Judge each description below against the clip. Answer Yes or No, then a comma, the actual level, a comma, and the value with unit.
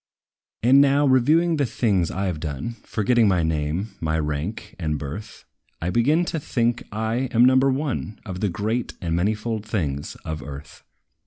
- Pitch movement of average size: No, wide, 7.2 semitones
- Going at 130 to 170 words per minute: Yes, average, 165 wpm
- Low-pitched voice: Yes, low, 105 Hz